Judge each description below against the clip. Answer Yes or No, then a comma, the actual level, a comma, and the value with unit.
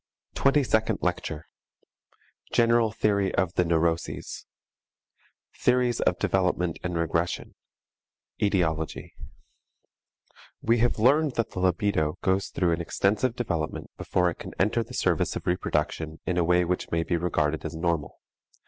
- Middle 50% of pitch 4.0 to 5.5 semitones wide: Yes, average, 4.8 semitones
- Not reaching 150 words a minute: Yes, slow, 135 wpm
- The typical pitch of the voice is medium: No, very low, 90 Hz